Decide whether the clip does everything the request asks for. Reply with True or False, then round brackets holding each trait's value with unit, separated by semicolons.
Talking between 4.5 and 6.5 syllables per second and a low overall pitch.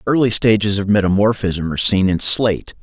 True (5.7 syllables/s; 100 Hz)